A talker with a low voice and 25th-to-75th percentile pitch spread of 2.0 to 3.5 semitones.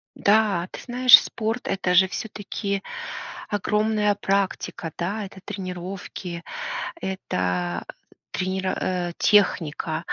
No: high, 190 Hz; average, 2.8 semitones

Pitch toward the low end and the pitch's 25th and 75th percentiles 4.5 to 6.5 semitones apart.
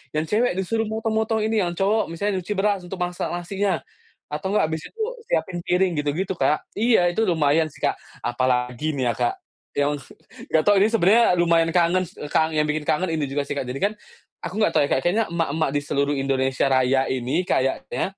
No: medium, 170 Hz; wide, 5.5 semitones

